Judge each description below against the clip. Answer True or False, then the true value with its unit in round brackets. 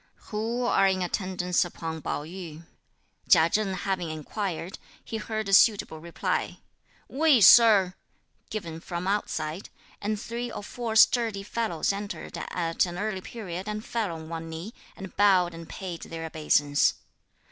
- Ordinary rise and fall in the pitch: True (4.3 semitones)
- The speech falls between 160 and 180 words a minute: False (145 wpm)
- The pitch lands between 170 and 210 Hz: True (190 Hz)